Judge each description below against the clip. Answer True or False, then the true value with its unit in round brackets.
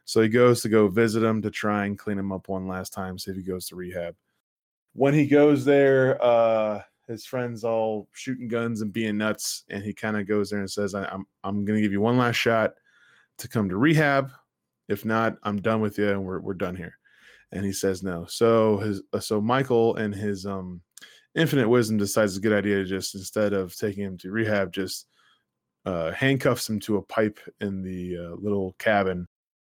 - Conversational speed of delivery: False (215 wpm)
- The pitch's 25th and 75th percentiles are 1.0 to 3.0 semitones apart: True (2.7 semitones)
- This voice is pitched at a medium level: False (105 Hz)